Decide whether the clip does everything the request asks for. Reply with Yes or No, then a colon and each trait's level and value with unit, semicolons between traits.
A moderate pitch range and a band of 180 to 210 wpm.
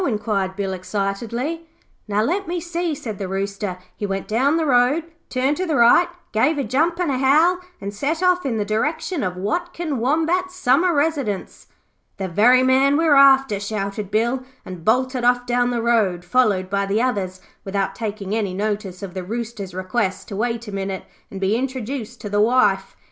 No: wide, 5.8 semitones; average, 185 wpm